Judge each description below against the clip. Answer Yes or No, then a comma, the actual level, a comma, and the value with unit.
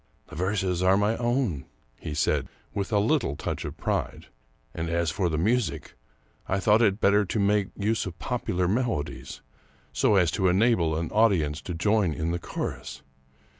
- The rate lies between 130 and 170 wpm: No, average, 180 wpm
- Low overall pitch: Yes, very low, 95 Hz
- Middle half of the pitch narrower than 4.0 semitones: No, average, 4.3 semitones